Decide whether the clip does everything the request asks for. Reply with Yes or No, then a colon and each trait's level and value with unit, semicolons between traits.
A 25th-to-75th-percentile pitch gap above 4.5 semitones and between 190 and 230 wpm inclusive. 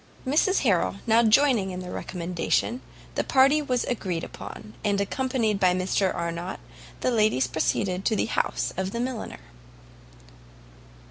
No: wide, 5.5 semitones; average, 140 wpm